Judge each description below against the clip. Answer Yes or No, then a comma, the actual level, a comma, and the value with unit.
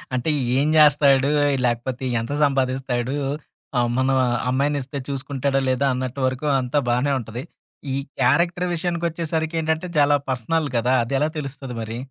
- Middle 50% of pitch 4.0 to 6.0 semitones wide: No, average, 2.9 semitones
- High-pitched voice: No, low, 135 Hz